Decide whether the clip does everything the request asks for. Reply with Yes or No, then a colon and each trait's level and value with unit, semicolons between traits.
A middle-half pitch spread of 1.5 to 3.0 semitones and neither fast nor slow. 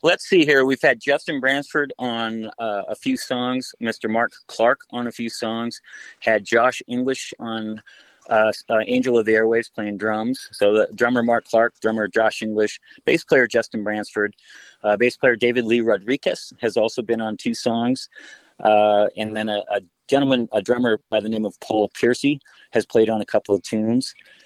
Yes: narrow, 2.6 semitones; average, 185 wpm